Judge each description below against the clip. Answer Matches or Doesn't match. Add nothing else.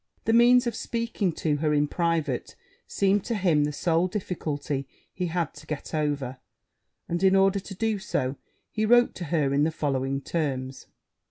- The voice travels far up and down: Doesn't match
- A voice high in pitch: Doesn't match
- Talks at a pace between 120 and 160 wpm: Doesn't match